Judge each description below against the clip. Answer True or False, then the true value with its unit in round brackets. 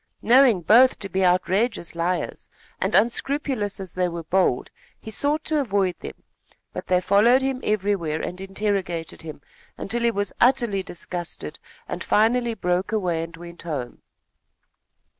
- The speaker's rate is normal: True (145 wpm)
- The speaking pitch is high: True (195 Hz)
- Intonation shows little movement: False (4.9 semitones)